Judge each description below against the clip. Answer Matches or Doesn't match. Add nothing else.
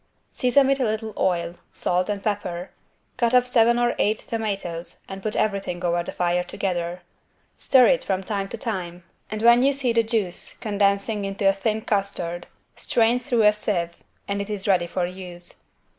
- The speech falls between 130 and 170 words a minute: Doesn't match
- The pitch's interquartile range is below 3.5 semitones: Doesn't match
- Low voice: Doesn't match